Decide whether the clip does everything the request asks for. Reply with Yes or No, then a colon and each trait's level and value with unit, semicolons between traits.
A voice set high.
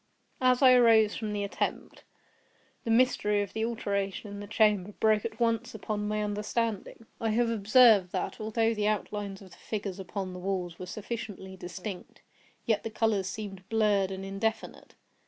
Yes: high, 210 Hz